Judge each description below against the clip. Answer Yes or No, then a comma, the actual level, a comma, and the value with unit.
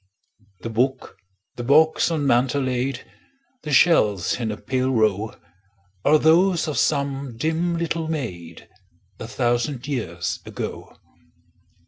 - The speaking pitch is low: Yes, low, 130 Hz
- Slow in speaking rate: Yes, slow, 120 wpm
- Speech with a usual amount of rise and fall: Yes, average, 5.0 semitones